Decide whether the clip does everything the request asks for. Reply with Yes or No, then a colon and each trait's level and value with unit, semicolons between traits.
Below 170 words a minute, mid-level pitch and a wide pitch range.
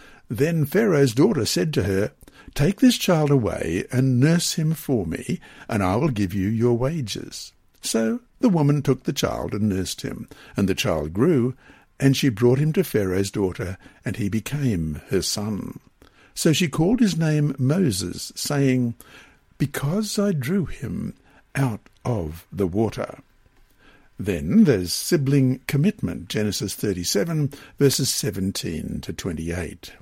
No: average, 150 wpm; low, 130 Hz; wide, 6.7 semitones